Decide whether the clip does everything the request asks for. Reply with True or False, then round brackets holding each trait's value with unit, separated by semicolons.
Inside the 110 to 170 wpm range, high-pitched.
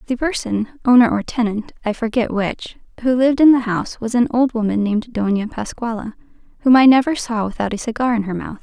False (195 wpm; 230 Hz)